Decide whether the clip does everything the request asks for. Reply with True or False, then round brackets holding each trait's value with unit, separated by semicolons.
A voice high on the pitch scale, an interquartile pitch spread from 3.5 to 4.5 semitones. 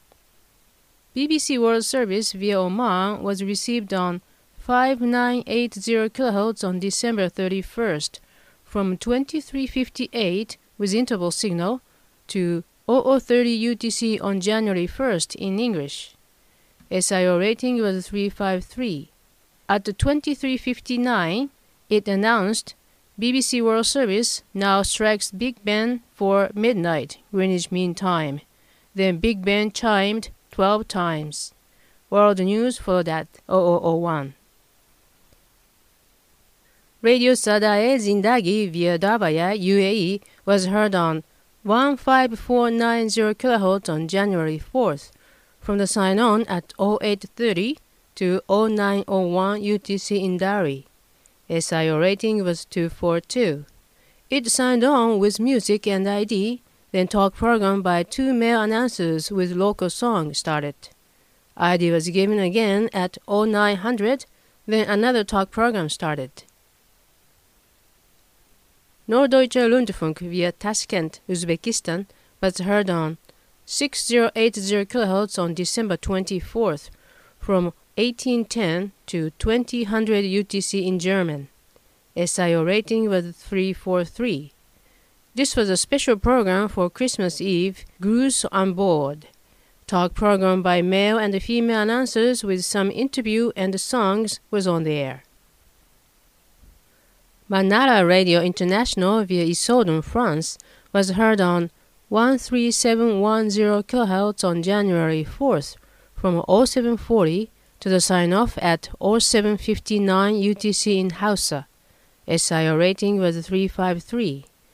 True (200 Hz; 4.1 semitones)